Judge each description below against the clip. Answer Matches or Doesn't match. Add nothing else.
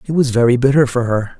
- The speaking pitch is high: Doesn't match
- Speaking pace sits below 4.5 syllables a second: Doesn't match